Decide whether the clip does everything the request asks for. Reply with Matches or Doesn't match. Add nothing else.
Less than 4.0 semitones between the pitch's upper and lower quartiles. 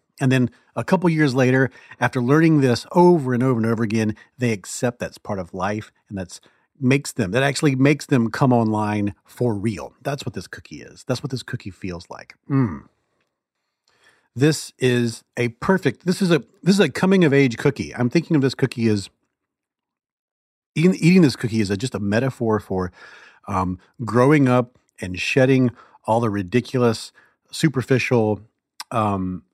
Doesn't match